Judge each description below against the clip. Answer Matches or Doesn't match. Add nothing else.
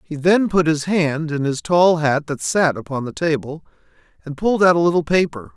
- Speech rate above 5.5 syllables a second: Doesn't match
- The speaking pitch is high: Doesn't match